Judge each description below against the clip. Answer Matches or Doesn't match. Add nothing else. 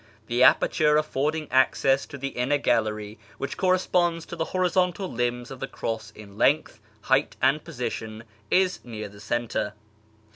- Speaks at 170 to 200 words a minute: Doesn't match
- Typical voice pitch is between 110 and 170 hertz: Matches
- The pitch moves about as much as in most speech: Doesn't match